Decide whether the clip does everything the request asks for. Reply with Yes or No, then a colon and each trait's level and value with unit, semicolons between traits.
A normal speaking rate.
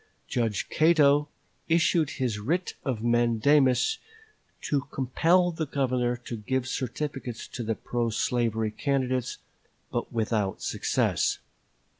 No: slow, 110 wpm